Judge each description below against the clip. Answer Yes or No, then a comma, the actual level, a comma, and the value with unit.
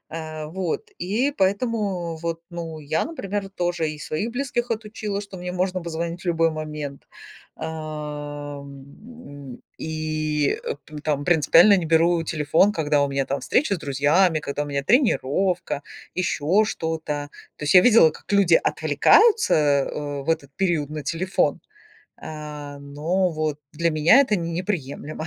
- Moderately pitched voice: Yes, medium, 160 Hz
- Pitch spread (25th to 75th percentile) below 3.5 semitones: No, average, 4.1 semitones